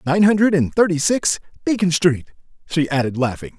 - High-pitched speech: No, medium, 165 Hz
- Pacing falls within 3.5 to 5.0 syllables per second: No, 5.4 syllables/s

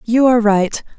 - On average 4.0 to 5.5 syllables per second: Yes, 5.2 syllables/s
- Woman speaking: Yes, female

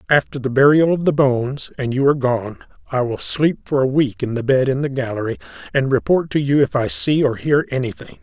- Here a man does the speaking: Yes, male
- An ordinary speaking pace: No, fast, 235 wpm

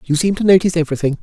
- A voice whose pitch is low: No, medium, 170 Hz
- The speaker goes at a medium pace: No, fast, 245 wpm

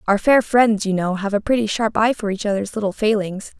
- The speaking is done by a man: No, female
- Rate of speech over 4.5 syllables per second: Yes, 5.6 syllables/s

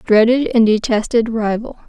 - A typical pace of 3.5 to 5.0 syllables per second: Yes, 4.5 syllables/s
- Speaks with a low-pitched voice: No, high, 225 Hz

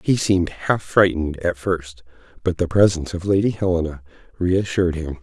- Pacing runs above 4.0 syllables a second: Yes, 5.5 syllables/s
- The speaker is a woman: No, male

